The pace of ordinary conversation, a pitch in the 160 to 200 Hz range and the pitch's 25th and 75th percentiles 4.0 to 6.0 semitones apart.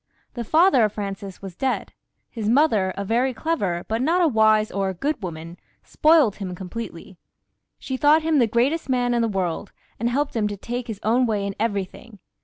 No: average, 195 wpm; high, 225 Hz; average, 4.8 semitones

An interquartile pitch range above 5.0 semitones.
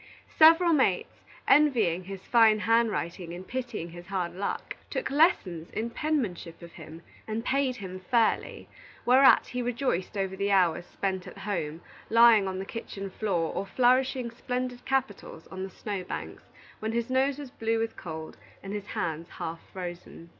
Yes: wide, 5.6 semitones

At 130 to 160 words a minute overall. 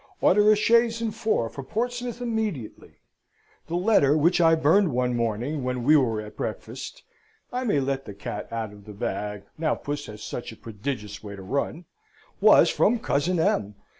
No: average, 180 wpm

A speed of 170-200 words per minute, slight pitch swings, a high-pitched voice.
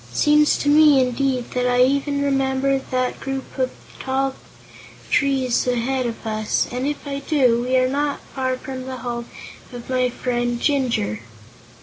No: average, 160 wpm; narrow, 1.8 semitones; very high, 260 Hz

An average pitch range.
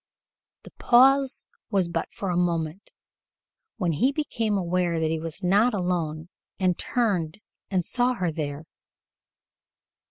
Yes: average, 4.9 semitones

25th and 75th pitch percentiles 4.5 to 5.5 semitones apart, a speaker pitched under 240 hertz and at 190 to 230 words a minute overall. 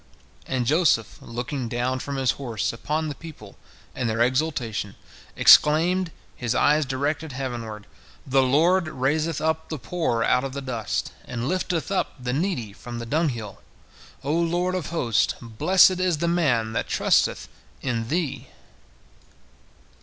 No: average, 5.2 semitones; low, 135 Hz; average, 145 wpm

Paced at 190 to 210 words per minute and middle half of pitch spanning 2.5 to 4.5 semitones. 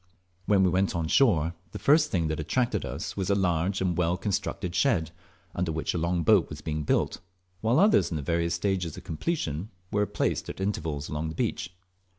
Yes: average, 195 wpm; average, 3.8 semitones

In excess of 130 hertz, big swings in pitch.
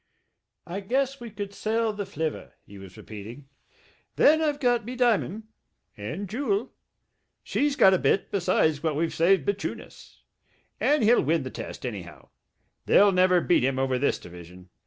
Yes: high, 190 Hz; wide, 9.0 semitones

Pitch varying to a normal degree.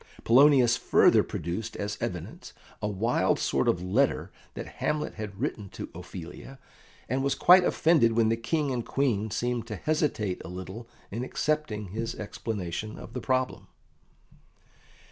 Yes: average, 4.6 semitones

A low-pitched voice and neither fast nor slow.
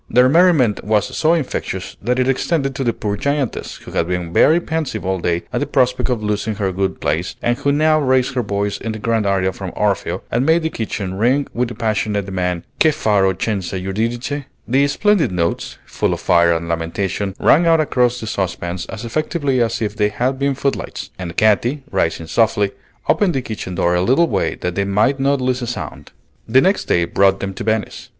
No: low, 110 Hz; fast, 210 wpm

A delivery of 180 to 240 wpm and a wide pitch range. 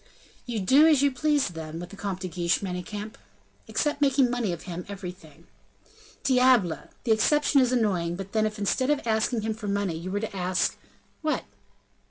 Yes: average, 190 wpm; wide, 5.9 semitones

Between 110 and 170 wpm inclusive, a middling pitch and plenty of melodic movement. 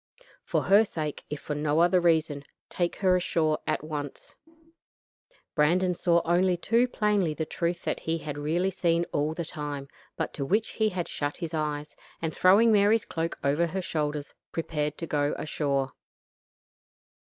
No: average, 165 wpm; medium, 165 Hz; average, 3.3 semitones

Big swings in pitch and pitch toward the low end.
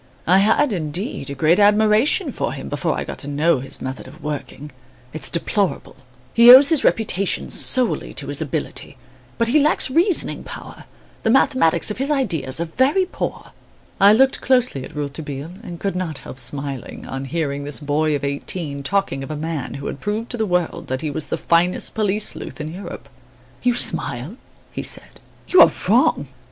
No: wide, 7.5 semitones; medium, 170 Hz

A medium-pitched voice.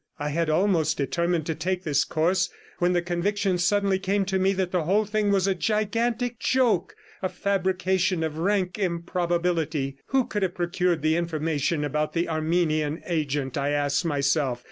Yes: medium, 175 Hz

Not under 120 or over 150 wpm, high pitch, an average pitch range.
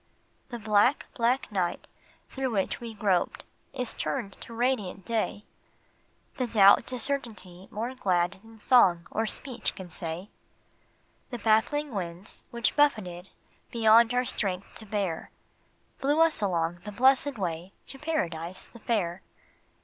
Yes: slow, 135 wpm; high, 215 Hz; average, 4.9 semitones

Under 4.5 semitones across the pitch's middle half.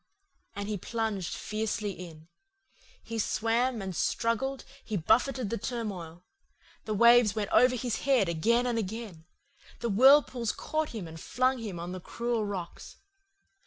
Yes: average, 3.7 semitones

